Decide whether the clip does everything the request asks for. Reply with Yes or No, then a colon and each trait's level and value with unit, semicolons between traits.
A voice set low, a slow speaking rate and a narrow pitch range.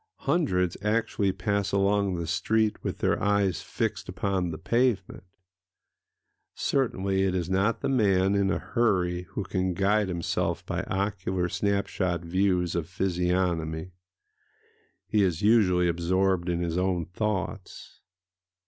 Yes: very low, 95 Hz; slow, 130 wpm; narrow, 2.3 semitones